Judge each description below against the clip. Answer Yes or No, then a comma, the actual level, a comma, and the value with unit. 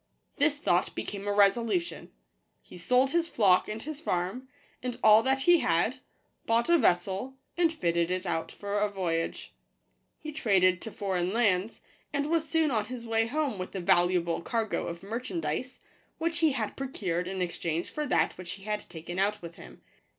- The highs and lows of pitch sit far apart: Yes, wide, 6.7 semitones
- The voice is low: No, high, 210 Hz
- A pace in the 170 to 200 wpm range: Yes, average, 180 wpm